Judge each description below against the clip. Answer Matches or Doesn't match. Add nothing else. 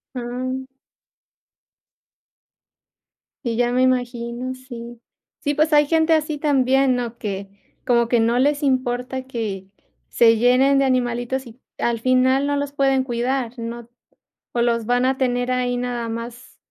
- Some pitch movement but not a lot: Doesn't match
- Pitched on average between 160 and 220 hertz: Doesn't match